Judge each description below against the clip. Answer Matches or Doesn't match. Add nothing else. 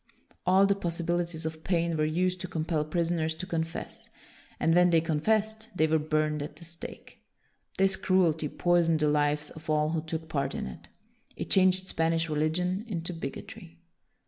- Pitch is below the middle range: Doesn't match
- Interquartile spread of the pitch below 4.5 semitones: Matches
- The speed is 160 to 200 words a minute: Matches